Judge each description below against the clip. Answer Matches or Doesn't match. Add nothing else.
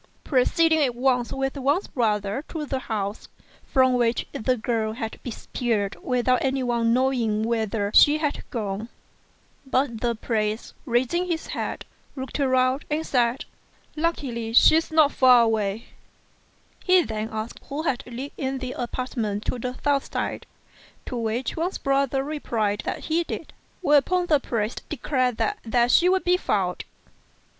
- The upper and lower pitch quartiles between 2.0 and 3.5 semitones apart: Doesn't match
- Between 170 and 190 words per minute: Doesn't match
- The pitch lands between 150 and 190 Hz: Doesn't match